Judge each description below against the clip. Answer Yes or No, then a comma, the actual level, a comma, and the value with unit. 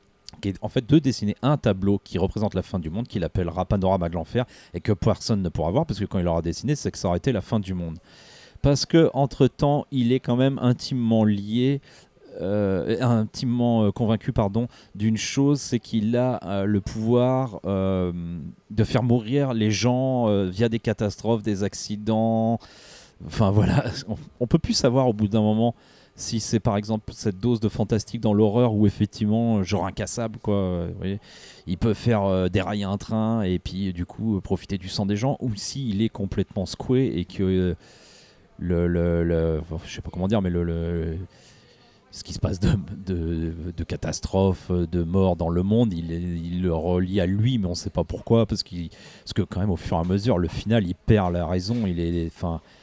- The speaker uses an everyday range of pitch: Yes, average, 4.2 semitones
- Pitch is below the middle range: Yes, low, 105 Hz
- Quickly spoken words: No, average, 205 wpm